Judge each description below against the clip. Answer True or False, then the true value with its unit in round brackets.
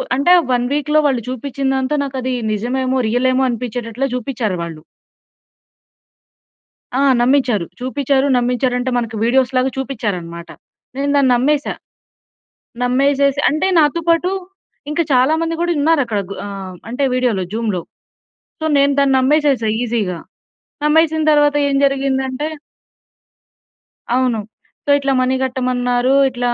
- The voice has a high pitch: True (260 Hz)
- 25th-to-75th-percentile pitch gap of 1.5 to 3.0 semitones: True (2.5 semitones)